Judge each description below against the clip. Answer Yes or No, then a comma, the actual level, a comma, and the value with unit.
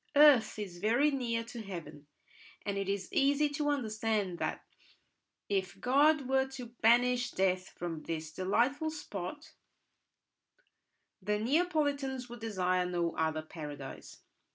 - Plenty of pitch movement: Yes, wide, 6.6 semitones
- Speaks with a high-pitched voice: Yes, high, 225 Hz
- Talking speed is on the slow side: Yes, slow, 125 wpm